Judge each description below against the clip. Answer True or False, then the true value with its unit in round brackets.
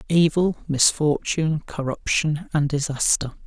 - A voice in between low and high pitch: True (150 Hz)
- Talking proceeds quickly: False (85 wpm)